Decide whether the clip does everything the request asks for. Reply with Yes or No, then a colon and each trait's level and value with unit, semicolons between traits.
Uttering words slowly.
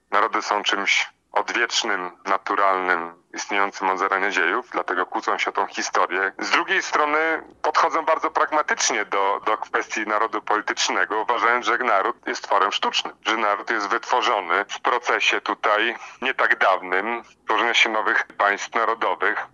No: average, 145 wpm